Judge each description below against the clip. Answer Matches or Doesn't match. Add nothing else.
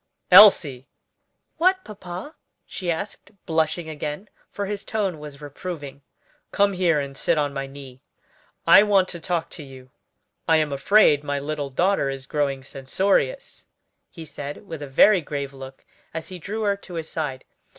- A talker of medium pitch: Matches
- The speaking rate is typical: Matches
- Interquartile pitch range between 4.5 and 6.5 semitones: Matches